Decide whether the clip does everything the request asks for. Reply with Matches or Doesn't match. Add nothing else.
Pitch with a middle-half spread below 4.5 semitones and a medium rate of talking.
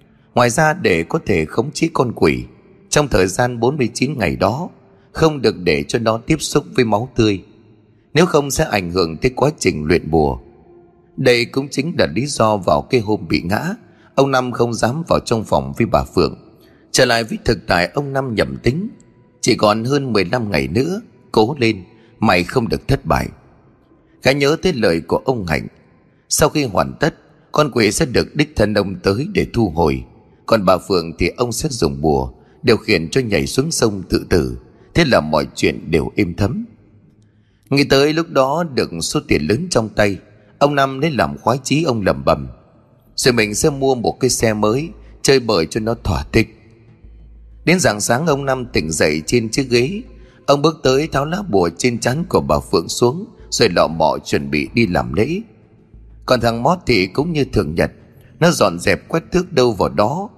Doesn't match